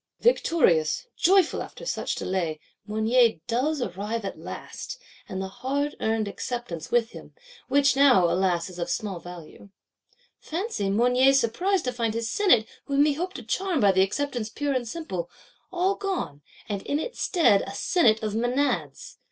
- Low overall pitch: No, high, 235 Hz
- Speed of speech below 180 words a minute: Yes, average, 160 wpm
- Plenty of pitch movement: Yes, wide, 6.7 semitones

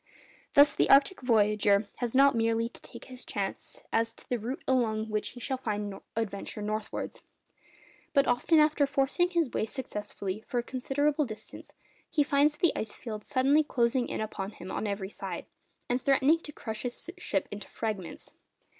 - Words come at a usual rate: Yes, average, 170 wpm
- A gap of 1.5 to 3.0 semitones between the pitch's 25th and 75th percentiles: No, average, 4.6 semitones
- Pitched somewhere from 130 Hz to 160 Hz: No, high, 245 Hz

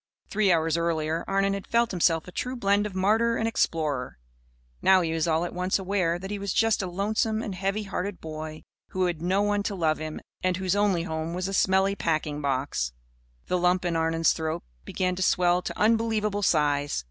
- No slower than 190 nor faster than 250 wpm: Yes, fast, 205 wpm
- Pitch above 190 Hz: No, medium, 180 Hz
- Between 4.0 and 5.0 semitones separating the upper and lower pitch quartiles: No, average, 3.6 semitones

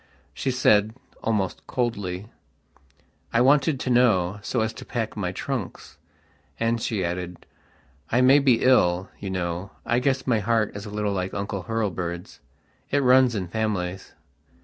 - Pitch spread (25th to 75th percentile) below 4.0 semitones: No, average, 4.7 semitones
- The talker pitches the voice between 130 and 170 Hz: No, low, 110 Hz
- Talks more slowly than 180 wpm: Yes, average, 150 wpm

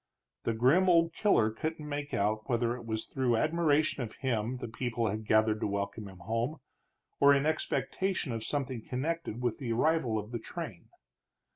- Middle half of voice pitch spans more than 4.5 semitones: Yes, average, 5.3 semitones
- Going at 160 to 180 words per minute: Yes, average, 175 wpm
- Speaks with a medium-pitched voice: No, low, 120 Hz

